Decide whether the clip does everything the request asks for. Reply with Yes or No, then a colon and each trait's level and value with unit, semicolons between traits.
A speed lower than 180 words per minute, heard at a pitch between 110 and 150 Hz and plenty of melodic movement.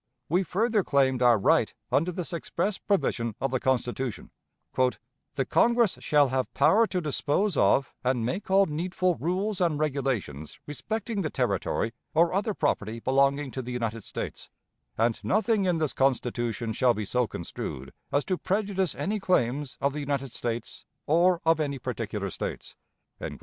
Yes: average, 155 wpm; medium, 140 Hz; wide, 6.9 semitones